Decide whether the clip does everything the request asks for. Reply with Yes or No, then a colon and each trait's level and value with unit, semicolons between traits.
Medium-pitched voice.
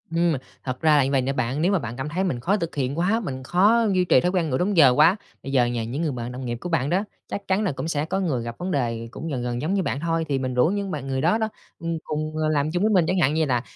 Yes: medium, 155 Hz